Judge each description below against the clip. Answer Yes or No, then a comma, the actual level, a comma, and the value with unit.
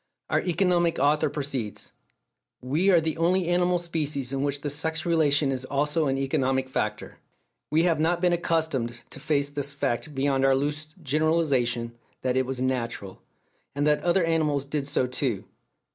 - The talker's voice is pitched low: No, medium, 145 Hz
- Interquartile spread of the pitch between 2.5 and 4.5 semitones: Yes, average, 3.4 semitones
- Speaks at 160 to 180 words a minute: Yes, average, 165 wpm